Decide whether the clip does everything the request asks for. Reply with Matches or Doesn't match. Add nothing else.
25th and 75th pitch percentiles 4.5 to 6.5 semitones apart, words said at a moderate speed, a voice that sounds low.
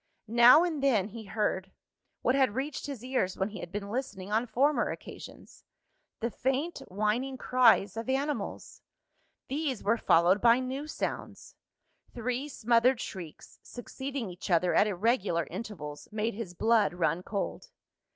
Doesn't match